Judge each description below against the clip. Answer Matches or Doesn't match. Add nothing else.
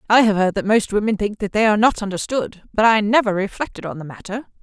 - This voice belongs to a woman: Matches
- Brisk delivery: Matches